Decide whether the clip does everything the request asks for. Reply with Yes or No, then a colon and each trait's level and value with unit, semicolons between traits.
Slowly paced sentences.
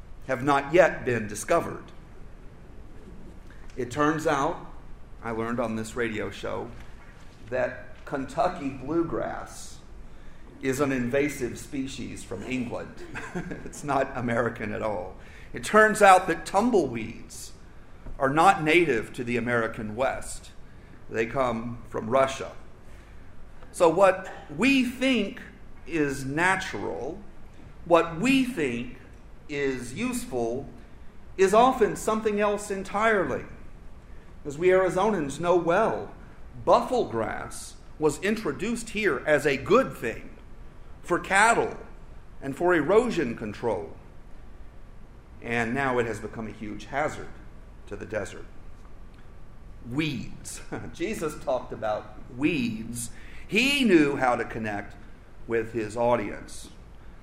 Yes: slow, 110 wpm